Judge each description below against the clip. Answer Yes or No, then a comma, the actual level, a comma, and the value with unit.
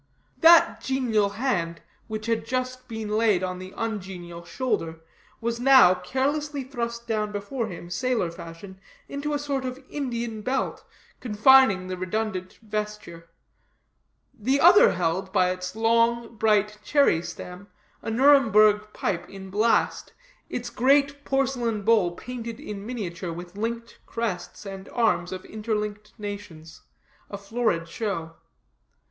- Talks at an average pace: No, slow, 130 wpm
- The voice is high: Yes, high, 215 Hz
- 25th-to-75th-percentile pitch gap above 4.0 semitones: Yes, average, 4.7 semitones